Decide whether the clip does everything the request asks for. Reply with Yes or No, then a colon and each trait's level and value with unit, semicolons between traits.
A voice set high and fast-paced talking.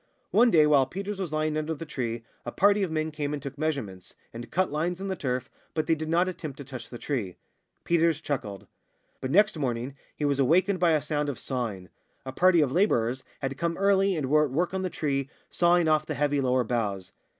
No: medium, 150 Hz; fast, 225 wpm